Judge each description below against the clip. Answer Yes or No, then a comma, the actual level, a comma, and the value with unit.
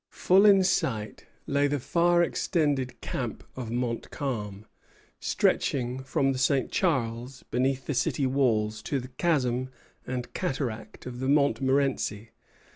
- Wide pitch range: No, average, 2.8 semitones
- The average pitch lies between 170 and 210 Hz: No, low, 130 Hz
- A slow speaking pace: Yes, slow, 125 wpm